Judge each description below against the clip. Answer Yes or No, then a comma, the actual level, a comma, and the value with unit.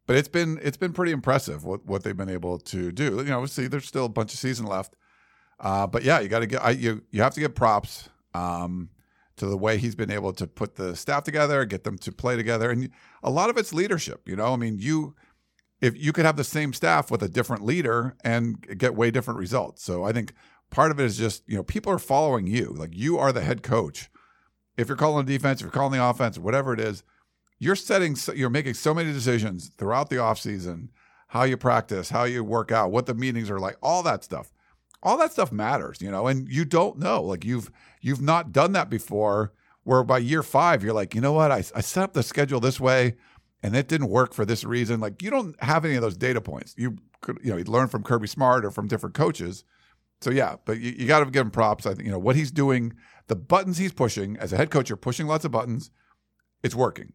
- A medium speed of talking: No, fast, 250 wpm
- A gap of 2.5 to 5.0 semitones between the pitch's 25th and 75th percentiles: Yes, average, 4.5 semitones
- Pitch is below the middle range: Yes, low, 125 Hz